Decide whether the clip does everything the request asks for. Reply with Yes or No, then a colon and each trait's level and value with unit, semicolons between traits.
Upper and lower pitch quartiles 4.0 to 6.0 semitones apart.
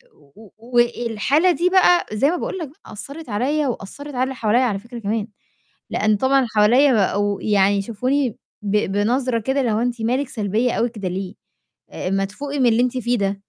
Yes: average, 4.3 semitones